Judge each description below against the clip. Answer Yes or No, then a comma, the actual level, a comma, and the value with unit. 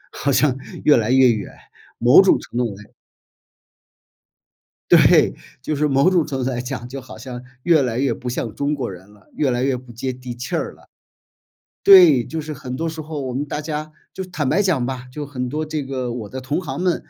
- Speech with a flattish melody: No, average, 3.5 semitones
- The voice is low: Yes, low, 130 Hz